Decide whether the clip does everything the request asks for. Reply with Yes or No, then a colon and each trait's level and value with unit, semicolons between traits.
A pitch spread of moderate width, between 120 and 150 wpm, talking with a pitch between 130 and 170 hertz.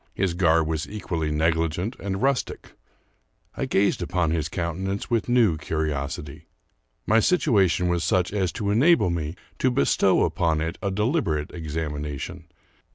No: average, 4.2 semitones; average, 140 wpm; very low, 85 Hz